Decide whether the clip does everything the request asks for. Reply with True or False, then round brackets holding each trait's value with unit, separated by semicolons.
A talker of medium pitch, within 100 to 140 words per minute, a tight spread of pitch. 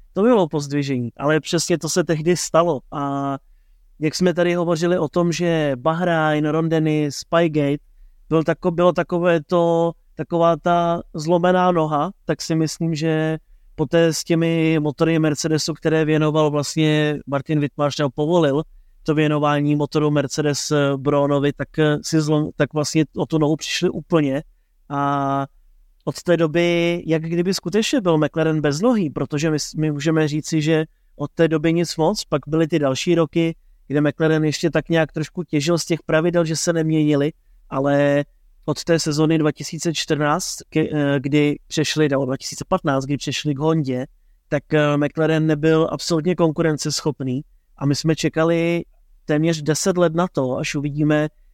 False (155 Hz; 150 wpm; 2.2 semitones)